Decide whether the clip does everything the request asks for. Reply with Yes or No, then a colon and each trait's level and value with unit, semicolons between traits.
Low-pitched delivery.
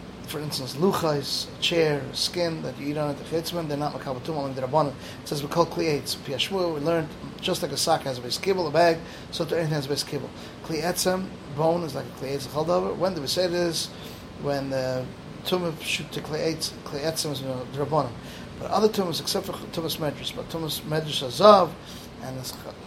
No: medium, 155 Hz